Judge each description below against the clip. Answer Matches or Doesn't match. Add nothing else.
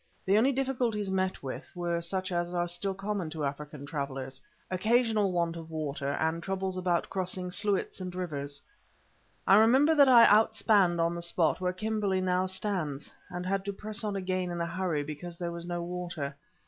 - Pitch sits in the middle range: Matches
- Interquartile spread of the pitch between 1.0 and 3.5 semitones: Matches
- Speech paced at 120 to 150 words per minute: Doesn't match